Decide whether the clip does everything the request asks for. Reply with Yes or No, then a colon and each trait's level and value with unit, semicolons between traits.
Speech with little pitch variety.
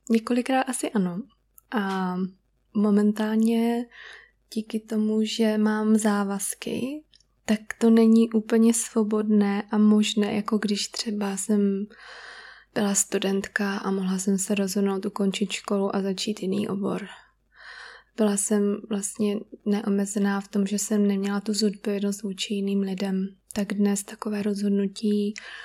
Yes: narrow, 1.7 semitones